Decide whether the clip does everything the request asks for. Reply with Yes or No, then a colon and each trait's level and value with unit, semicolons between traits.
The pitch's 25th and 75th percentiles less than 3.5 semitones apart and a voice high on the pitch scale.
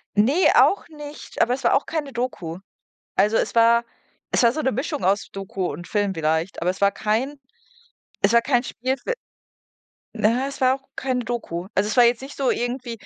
No: average, 5.0 semitones; high, 240 Hz